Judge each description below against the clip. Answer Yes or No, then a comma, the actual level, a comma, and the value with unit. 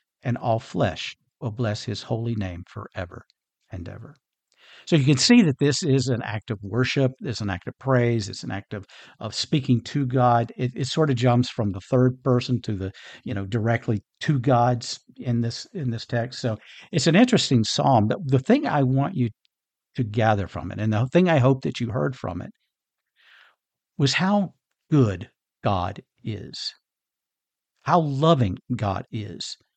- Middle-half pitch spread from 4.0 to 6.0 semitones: No, average, 3.6 semitones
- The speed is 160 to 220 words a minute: Yes, average, 180 wpm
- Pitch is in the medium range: No, low, 125 Hz